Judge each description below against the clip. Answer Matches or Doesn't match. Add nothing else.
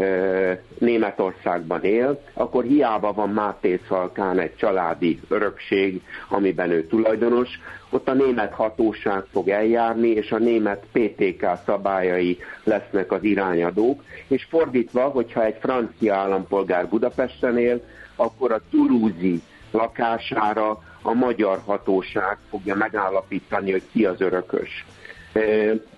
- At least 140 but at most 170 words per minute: Doesn't match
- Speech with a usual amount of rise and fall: Matches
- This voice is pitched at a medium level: Doesn't match